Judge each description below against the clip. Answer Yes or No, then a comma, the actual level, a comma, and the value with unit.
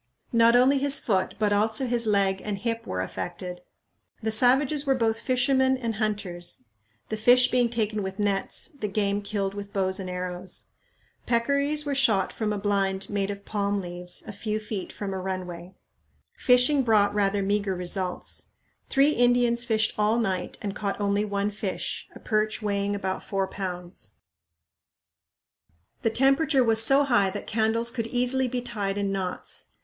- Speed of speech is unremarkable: Yes, average, 165 wpm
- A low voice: No, high, 210 Hz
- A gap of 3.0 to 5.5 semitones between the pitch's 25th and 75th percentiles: Yes, average, 3.6 semitones